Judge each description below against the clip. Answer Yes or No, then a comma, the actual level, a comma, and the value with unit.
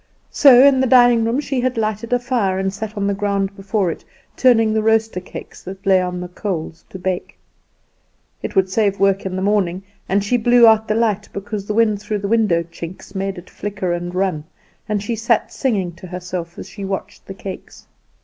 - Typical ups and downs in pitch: Yes, average, 3.0 semitones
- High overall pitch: Yes, high, 200 Hz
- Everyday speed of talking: No, fast, 210 wpm